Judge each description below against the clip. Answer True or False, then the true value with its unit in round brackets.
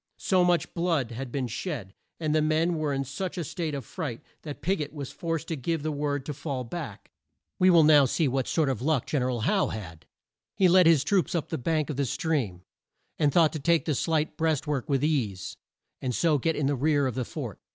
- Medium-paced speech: False (235 wpm)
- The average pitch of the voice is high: False (150 Hz)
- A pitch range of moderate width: True (3.7 semitones)